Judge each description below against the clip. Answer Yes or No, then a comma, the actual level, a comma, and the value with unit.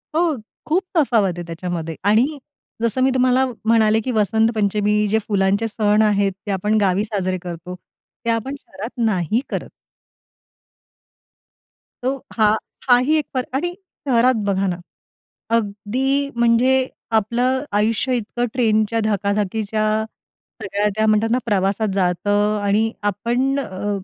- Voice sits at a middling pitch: No, high, 215 Hz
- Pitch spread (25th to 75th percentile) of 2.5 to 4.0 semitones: Yes, average, 3.3 semitones